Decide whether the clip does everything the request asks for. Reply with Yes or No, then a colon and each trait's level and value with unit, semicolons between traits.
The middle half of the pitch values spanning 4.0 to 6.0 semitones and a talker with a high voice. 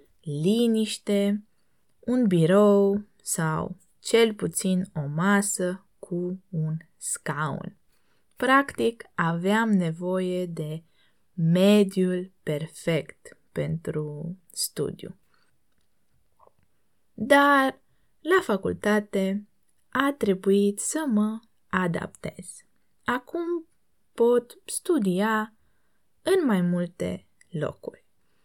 Yes: average, 4.4 semitones; high, 200 Hz